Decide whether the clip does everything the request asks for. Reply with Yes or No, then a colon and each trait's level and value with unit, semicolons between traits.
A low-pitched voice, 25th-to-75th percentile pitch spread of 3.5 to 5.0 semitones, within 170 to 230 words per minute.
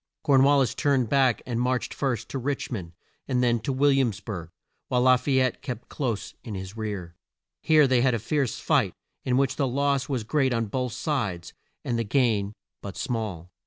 Yes: low, 125 Hz; average, 3.8 semitones; average, 200 wpm